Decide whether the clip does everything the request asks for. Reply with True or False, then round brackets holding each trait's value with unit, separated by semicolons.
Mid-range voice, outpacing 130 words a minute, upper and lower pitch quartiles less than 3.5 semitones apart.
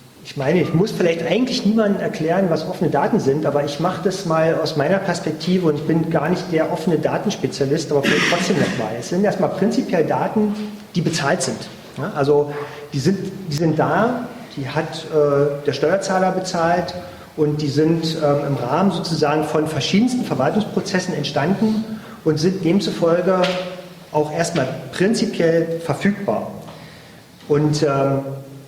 False (165 Hz; 150 wpm; 4.1 semitones)